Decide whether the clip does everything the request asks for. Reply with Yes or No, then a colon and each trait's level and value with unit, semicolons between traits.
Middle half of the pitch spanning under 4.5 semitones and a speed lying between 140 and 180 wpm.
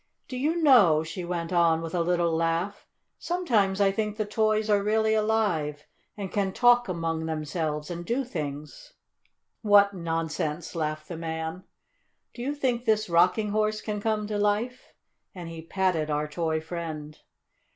No: average, 4.8 semitones; average, 160 wpm